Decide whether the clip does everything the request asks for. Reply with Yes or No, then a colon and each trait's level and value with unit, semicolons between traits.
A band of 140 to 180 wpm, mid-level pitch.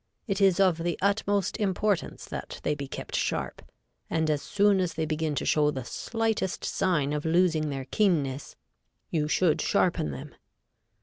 Yes: average, 165 wpm; medium, 165 Hz